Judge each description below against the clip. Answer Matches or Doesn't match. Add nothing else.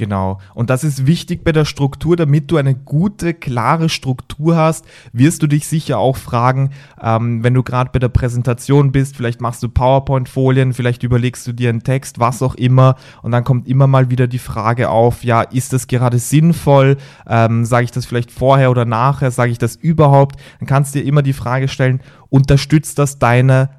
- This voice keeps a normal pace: Doesn't match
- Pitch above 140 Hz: Doesn't match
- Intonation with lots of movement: Doesn't match